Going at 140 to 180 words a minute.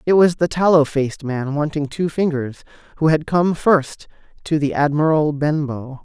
Yes: average, 170 wpm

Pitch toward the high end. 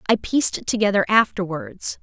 Yes: high, 205 Hz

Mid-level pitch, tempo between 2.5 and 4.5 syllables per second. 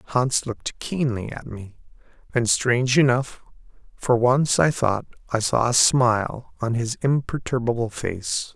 No: low, 120 Hz; 4.1 syllables/s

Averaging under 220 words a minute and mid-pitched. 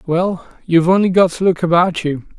Yes: average, 200 wpm; medium, 175 Hz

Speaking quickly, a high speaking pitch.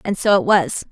Yes: fast, 260 wpm; high, 200 Hz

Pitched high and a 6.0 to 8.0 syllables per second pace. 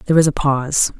No: medium, 145 Hz; 6.5 syllables/s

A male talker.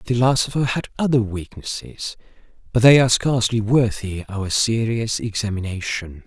Yes: male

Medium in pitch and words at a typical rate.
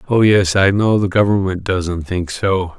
No: very low, 95 Hz; average, 195 wpm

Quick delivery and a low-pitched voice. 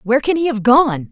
No: fast, 270 wpm; very high, 250 Hz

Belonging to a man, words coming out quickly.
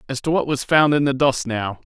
Yes: male; fast, 285 wpm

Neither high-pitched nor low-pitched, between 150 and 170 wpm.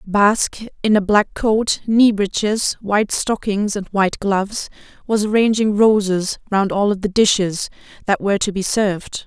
No: high, 205 Hz; average, 160 wpm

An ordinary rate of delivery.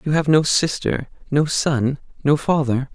No: slow, 120 wpm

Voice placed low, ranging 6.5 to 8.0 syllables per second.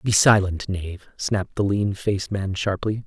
No: low, 100 Hz; 4.9 syllables/s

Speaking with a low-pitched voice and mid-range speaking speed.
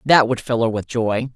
No: low, 120 Hz; fast, 265 wpm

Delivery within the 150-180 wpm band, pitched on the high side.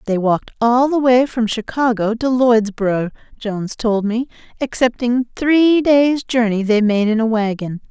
Yes: average, 160 wpm; high, 235 Hz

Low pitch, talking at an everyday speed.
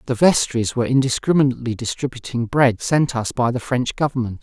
Yes: low, 125 Hz; average, 165 wpm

